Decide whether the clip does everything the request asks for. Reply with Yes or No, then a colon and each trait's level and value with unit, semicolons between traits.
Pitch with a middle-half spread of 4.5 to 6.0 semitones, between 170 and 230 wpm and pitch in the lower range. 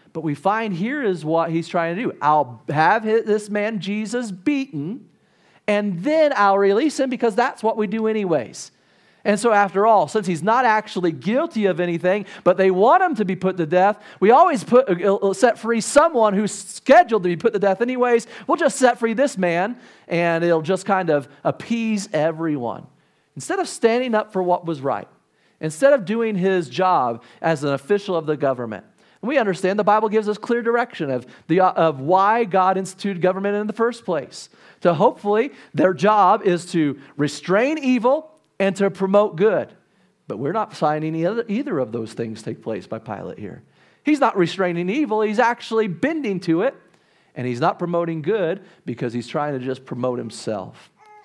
No: average, 5.1 semitones; average, 185 wpm; high, 195 Hz